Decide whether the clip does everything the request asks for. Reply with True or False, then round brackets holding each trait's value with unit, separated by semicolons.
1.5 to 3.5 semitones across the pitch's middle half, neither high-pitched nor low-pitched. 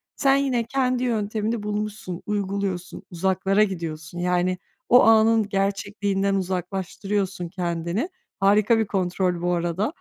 False (3.1 semitones; 195 Hz)